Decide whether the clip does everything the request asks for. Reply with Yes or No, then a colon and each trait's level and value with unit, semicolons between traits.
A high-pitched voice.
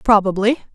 Yes: high, 210 Hz